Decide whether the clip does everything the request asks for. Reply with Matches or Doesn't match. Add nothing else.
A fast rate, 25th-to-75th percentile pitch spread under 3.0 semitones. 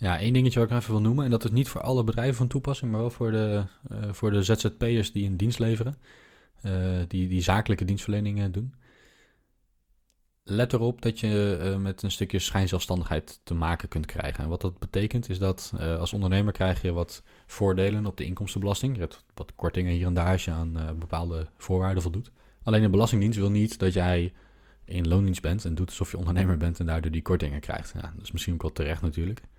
Doesn't match